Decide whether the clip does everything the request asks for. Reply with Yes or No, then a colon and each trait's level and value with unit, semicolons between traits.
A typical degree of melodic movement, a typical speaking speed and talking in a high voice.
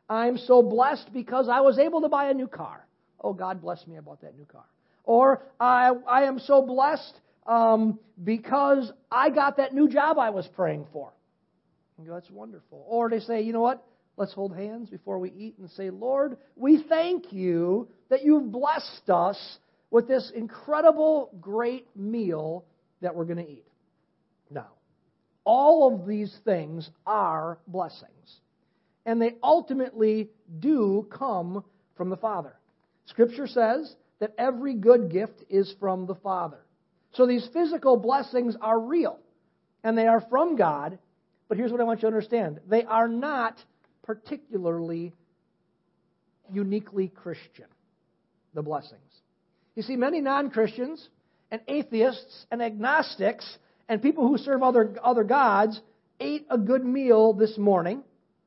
No: wide, 5.7 semitones; average, 150 wpm; high, 225 Hz